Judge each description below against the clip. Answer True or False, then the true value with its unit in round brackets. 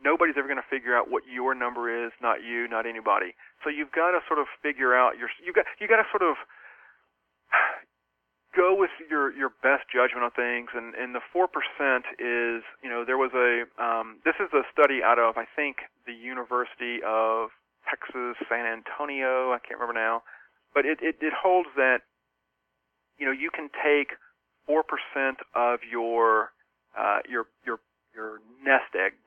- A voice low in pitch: True (120 Hz)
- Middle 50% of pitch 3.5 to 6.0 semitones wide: False (2.9 semitones)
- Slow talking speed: False (180 wpm)